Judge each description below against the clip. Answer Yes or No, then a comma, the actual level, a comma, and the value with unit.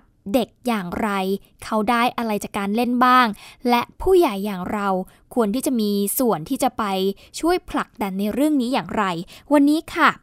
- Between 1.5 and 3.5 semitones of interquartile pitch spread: No, average, 4.3 semitones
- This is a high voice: Yes, high, 230 Hz